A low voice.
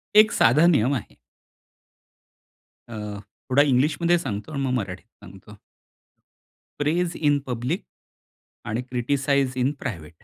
Yes: low, 130 Hz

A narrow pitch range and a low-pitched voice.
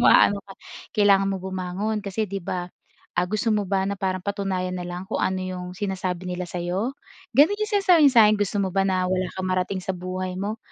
No: narrow, 1.9 semitones; high, 190 Hz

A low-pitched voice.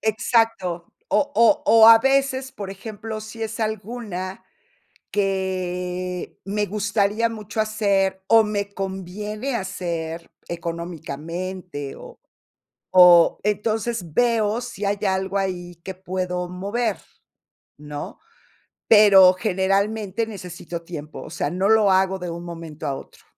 No: high, 195 Hz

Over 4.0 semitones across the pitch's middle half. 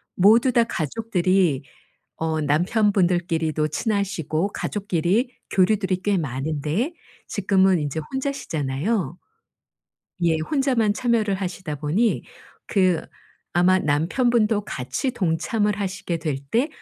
Yes: average, 5.2 semitones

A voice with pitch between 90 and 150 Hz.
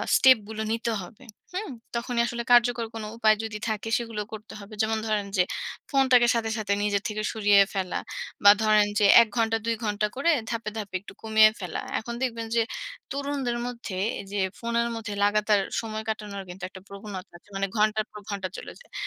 No: high, 220 Hz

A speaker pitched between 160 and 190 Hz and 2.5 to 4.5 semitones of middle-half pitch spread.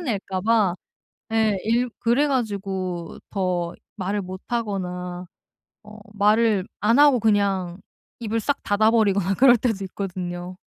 No: high, 205 Hz; average, 3.5 semitones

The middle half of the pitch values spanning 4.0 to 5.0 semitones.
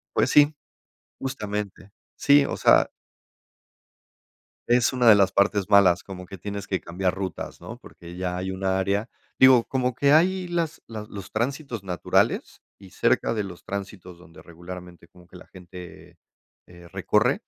Yes: average, 4.6 semitones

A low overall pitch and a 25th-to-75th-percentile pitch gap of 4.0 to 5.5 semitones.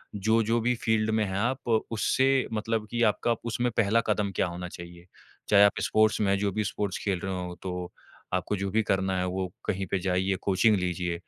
No: low, 100 Hz; average, 3.2 semitones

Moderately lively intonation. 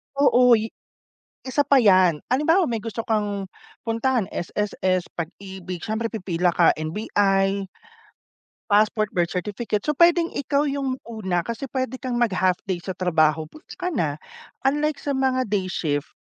No: wide, 5.9 semitones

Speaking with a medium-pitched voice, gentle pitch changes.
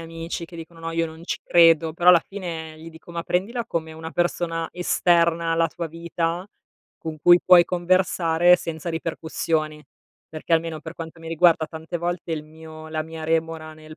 Yes: medium, 165 Hz; narrow, 1.2 semitones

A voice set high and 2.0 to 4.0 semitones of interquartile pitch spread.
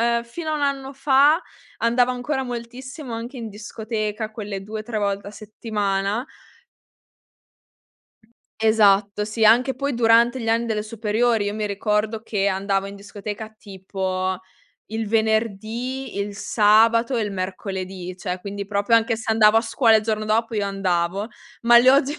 Yes: high, 220 Hz; average, 2.7 semitones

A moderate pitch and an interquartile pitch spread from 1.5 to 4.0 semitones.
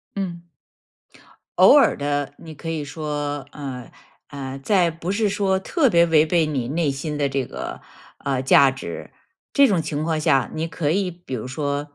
Yes: medium, 150 Hz; average, 3.4 semitones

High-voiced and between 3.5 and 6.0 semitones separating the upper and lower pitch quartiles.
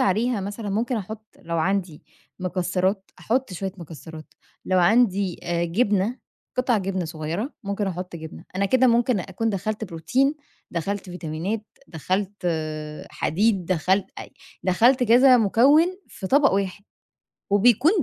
Yes: high, 195 Hz; average, 4.1 semitones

